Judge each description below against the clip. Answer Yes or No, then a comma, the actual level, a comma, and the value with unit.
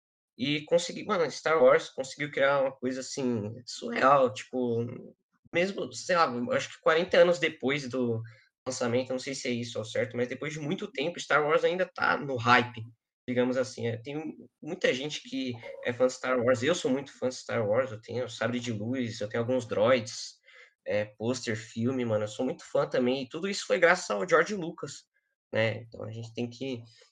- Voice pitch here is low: Yes, low, 125 Hz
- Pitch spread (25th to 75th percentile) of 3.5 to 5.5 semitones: No, average, 3.0 semitones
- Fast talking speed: Yes, fast, 200 wpm